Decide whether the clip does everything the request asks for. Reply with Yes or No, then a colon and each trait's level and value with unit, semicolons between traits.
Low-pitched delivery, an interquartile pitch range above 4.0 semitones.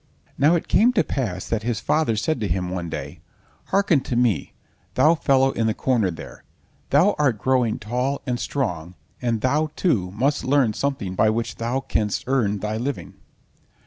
Yes: low, 120 Hz; average, 4.7 semitones